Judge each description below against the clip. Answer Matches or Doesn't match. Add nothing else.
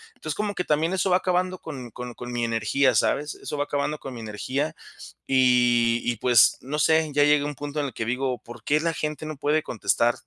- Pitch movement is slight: Doesn't match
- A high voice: Doesn't match